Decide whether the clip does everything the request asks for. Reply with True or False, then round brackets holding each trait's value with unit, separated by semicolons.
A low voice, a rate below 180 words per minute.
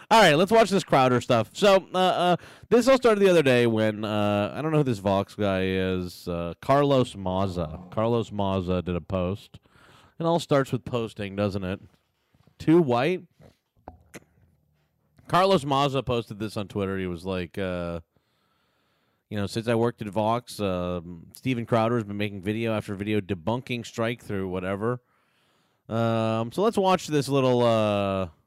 True (110 Hz; 170 wpm)